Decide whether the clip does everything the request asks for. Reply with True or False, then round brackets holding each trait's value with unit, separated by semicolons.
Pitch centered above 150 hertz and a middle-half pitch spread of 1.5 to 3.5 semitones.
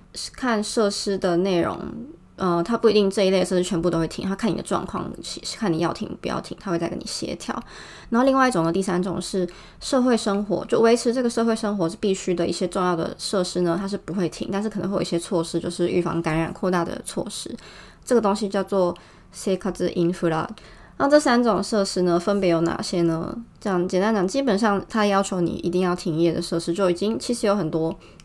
True (185 Hz; 3.1 semitones)